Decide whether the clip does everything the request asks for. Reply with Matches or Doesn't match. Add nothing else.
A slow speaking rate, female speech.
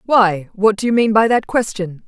Doesn't match